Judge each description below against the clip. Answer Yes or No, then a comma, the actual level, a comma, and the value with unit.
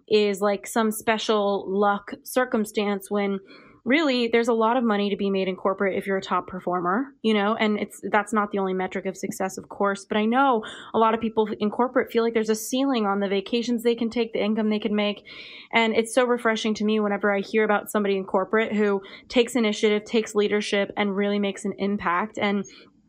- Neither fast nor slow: No, fast, 220 wpm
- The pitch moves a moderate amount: No, narrow, 2.3 semitones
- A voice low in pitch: No, high, 210 Hz